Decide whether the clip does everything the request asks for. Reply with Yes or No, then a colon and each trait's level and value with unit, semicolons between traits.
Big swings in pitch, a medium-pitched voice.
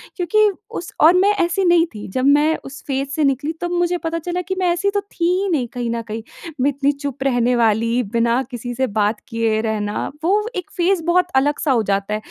No: wide, 6.9 semitones; very high, 280 Hz